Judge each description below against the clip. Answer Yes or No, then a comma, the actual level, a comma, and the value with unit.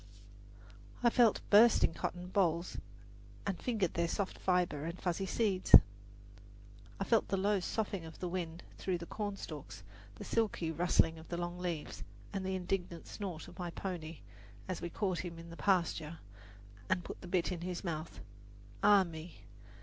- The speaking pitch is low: No, medium, 180 Hz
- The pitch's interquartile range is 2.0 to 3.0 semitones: Yes, narrow, 2.5 semitones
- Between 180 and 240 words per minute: No, average, 165 wpm